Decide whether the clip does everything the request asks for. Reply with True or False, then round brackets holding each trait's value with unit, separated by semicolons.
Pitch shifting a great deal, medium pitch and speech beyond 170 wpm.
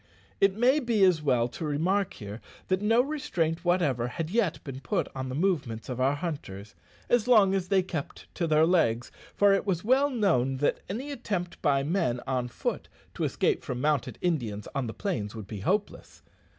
True (7.3 semitones; 165 Hz; 190 wpm)